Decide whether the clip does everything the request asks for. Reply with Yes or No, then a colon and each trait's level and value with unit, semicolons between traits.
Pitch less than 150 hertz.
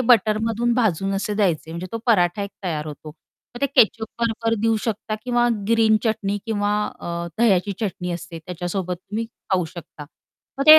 No: high, 205 Hz